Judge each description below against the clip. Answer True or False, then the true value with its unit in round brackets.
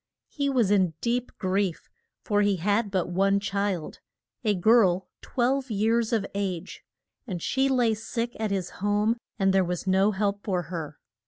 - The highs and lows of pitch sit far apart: False (3.1 semitones)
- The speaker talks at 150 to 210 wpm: True (165 wpm)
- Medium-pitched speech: False (200 Hz)